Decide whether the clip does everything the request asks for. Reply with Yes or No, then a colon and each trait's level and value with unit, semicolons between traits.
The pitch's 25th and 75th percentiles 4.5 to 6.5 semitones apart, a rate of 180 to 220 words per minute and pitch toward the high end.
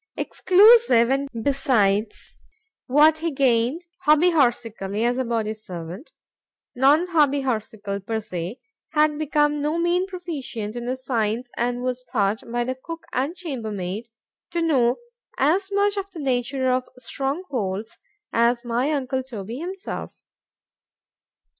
No: average, 5.0 semitones; slow, 135 wpm; very high, 260 Hz